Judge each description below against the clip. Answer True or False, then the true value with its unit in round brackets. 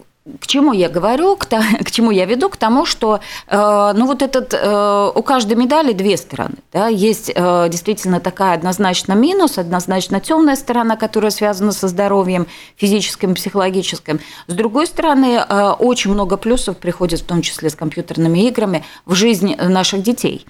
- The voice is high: True (205 Hz)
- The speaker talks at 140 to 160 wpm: True (155 wpm)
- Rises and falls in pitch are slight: False (4.0 semitones)